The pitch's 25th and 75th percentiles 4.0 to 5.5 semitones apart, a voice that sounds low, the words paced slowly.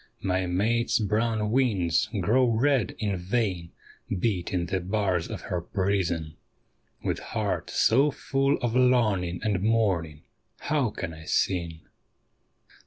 Yes: average, 4.7 semitones; low, 100 Hz; slow, 120 wpm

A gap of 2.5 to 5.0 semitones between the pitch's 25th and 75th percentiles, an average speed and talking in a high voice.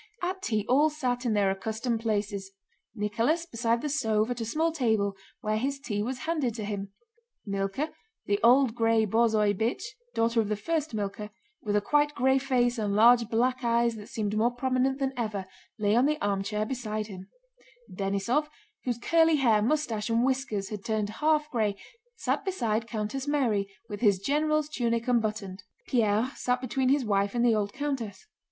Yes: average, 4.0 semitones; average, 175 wpm; high, 230 Hz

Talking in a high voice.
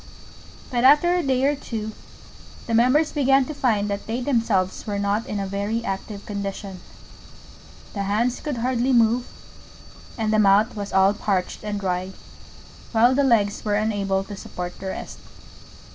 Yes: high, 215 Hz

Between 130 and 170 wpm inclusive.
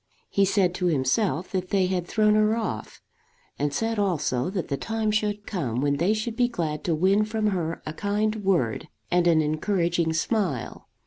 No: average, 185 wpm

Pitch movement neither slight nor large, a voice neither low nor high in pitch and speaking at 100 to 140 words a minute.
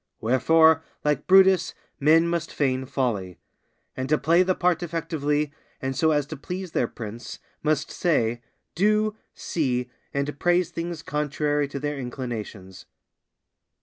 Yes: average, 4.3 semitones; medium, 150 Hz; slow, 135 wpm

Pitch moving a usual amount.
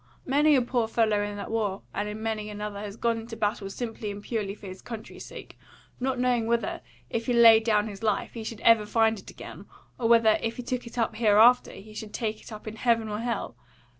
No: narrow, 2.0 semitones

